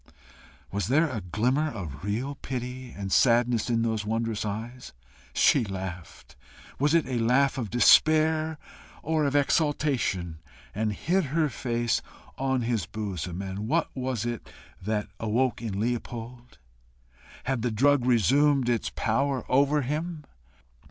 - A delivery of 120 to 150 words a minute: Yes, slow, 135 wpm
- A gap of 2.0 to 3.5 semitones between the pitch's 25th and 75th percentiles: No, average, 4.4 semitones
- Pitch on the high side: No, low, 120 Hz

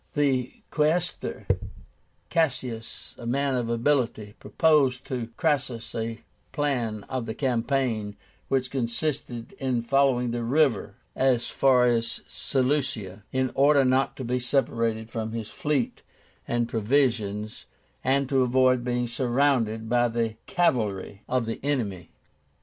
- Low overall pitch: Yes, low, 125 Hz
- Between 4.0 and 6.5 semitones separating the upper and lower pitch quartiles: No, average, 3.0 semitones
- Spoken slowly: Yes, slow, 125 wpm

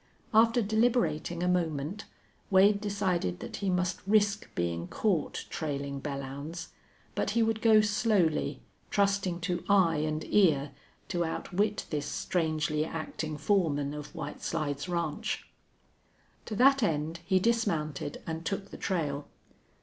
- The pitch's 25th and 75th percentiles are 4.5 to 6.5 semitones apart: Yes, average, 5.0 semitones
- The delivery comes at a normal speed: No, slow, 130 wpm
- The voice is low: No, medium, 175 Hz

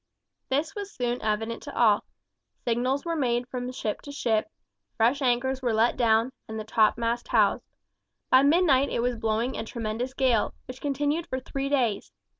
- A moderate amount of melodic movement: Yes, average, 3.1 semitones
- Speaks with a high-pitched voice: Yes, high, 245 Hz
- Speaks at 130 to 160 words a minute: No, average, 170 wpm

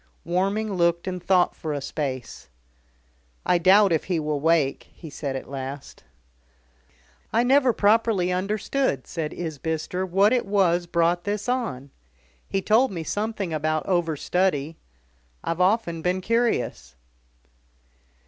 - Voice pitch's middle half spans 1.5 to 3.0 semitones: No, average, 4.5 semitones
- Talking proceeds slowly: Yes, slow, 130 wpm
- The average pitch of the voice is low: No, medium, 175 Hz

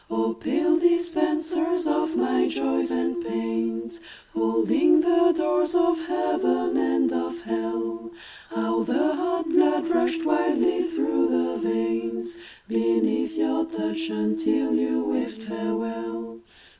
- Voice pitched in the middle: No, low, 115 Hz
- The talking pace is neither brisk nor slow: No, slow, 115 wpm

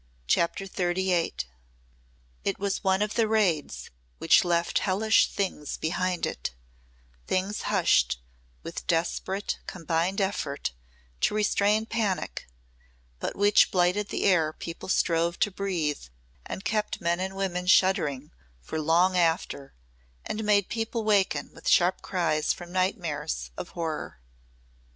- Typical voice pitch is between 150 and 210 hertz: Yes, medium, 185 Hz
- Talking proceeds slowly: Yes, slow, 125 wpm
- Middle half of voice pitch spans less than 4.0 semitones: Yes, average, 3.2 semitones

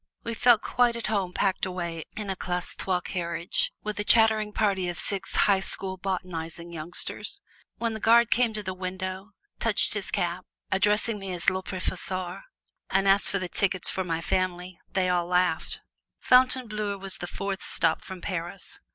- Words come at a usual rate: Yes, average, 175 wpm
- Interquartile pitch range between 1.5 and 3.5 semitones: Yes, average, 2.7 semitones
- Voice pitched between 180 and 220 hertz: Yes, high, 190 Hz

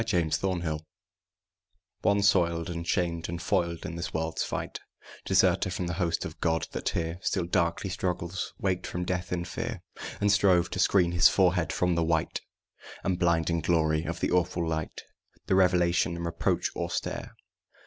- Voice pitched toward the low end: Yes, very low, 85 Hz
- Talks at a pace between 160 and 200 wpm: Yes, average, 170 wpm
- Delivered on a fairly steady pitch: Yes, narrow, 1.5 semitones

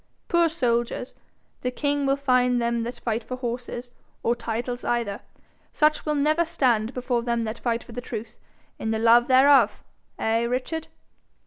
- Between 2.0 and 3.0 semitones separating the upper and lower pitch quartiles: Yes, narrow, 2.6 semitones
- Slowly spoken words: No, average, 160 wpm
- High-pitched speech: Yes, high, 245 Hz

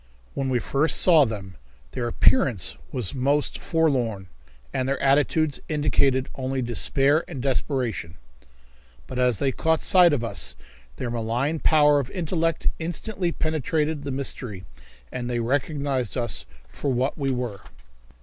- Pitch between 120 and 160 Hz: Yes, low, 135 Hz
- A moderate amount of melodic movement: Yes, average, 3.9 semitones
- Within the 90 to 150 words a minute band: Yes, average, 140 wpm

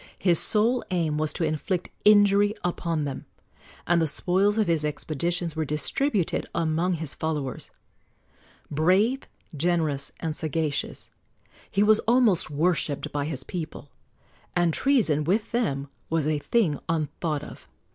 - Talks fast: No, slow, 135 wpm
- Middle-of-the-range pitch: Yes, medium, 165 Hz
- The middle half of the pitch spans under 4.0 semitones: No, average, 4.5 semitones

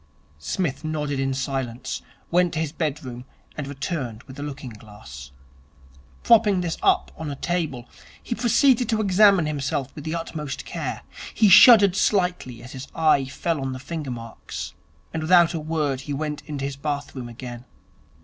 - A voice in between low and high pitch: Yes, medium, 150 Hz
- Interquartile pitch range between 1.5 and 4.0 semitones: No, average, 4.6 semitones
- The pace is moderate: Yes, average, 165 wpm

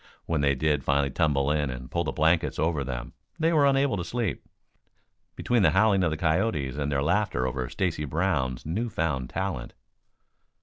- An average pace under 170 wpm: No, average, 180 wpm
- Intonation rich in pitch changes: Yes, wide, 5.7 semitones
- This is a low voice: Yes, very low, 80 Hz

